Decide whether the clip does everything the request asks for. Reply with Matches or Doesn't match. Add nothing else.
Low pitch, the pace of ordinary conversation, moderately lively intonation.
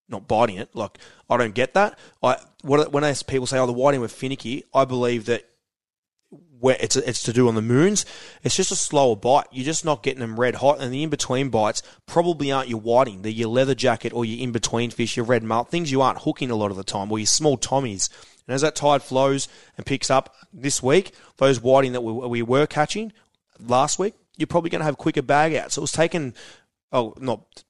Doesn't match